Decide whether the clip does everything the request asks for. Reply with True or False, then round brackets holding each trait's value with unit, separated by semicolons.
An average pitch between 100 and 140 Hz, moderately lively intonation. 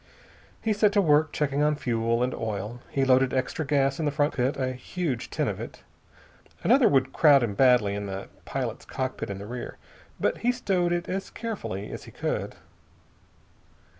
True (135 Hz; 4.6 semitones)